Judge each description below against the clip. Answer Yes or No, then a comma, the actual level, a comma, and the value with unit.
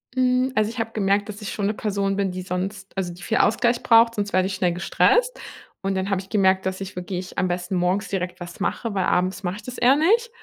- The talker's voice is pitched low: No, high, 195 Hz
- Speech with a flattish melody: No, average, 3.3 semitones